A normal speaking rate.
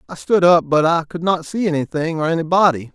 No: fast, 225 wpm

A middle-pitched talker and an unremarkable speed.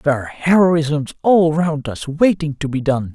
Yes: medium, 150 Hz; average, 190 wpm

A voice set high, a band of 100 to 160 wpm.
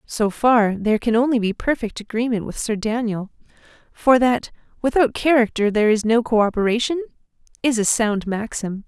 Yes: high, 230 Hz; average, 155 wpm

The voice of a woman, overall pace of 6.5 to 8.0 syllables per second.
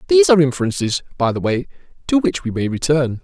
No: male; 6.8 syllables/s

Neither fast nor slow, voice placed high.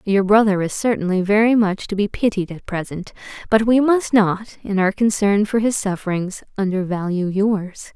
Yes: average, 175 wpm; high, 205 Hz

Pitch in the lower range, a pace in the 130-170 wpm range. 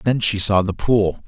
No: low, 105 Hz; fast, 235 wpm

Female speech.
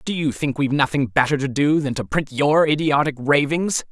No: male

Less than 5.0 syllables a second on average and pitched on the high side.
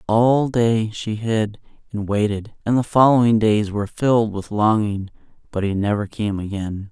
No: 4.6 syllables/s; low, 110 Hz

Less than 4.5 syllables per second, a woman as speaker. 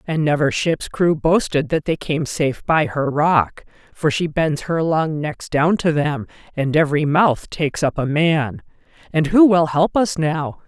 Yes: 4.2 syllables/s; female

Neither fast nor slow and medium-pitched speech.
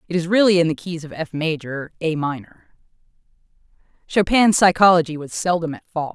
Yes: average, 155 wpm; medium, 165 Hz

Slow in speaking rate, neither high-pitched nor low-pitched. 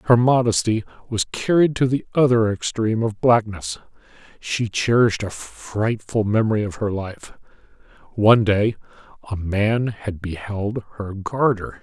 No: slow, 130 wpm; low, 110 Hz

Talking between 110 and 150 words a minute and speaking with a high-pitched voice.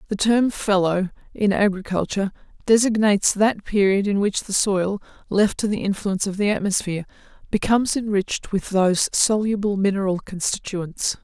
Yes: average, 140 wpm; high, 200 Hz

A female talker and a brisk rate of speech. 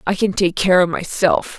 Yes: female; fast, 225 wpm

